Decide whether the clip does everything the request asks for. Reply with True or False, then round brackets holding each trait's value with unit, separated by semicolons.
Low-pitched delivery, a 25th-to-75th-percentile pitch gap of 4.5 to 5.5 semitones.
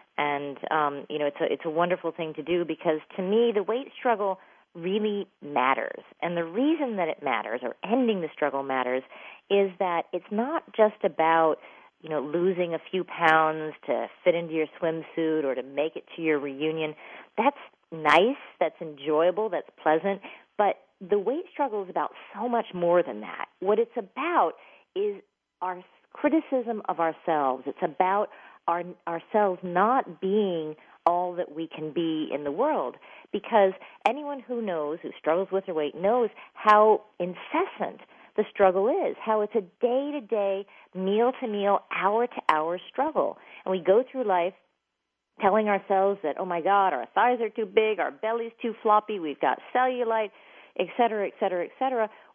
False (185 Hz; 5.1 semitones)